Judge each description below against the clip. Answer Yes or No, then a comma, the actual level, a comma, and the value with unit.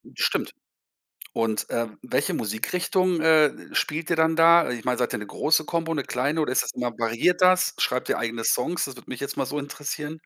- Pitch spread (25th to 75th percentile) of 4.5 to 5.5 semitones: Yes, average, 4.9 semitones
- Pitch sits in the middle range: Yes, medium, 150 Hz